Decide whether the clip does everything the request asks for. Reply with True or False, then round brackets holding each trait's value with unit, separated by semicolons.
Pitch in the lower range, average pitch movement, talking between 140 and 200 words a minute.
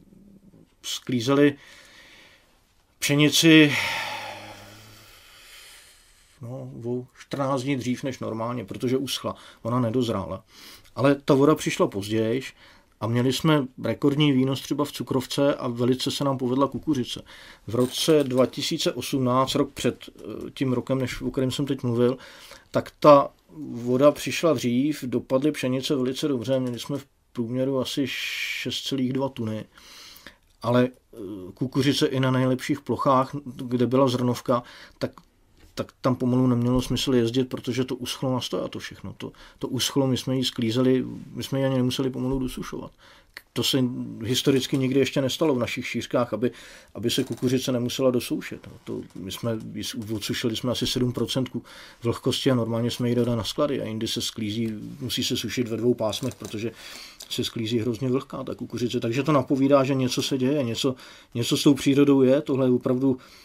False (130 Hz; 2.3 semitones; 150 wpm)